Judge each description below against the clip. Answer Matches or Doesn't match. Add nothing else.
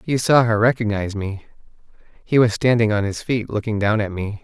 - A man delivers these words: Matches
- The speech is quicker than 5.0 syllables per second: Matches